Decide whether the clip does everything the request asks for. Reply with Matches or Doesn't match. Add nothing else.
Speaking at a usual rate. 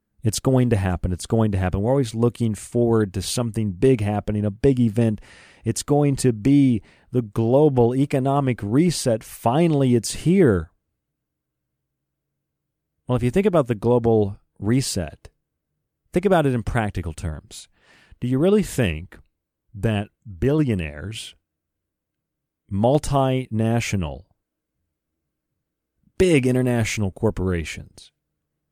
Doesn't match